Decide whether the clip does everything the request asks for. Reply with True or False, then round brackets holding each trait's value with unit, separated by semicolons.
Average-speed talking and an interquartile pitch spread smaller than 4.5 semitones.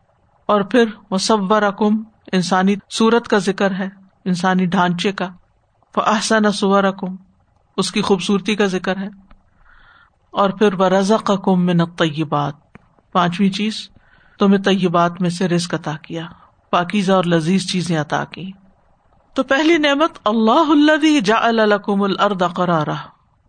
True (125 wpm; 2.8 semitones)